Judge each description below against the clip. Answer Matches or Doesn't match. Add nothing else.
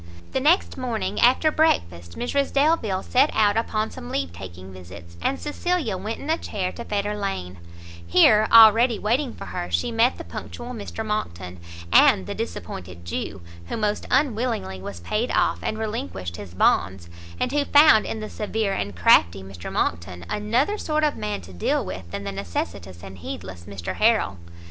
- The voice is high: Matches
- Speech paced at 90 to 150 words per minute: Doesn't match